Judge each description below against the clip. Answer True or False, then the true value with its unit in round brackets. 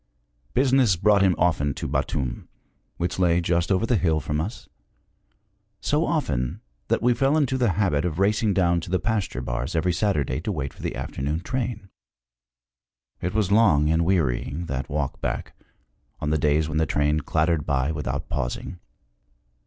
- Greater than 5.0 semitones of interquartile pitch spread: True (5.6 semitones)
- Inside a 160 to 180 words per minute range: True (170 wpm)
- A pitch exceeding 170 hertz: False (85 Hz)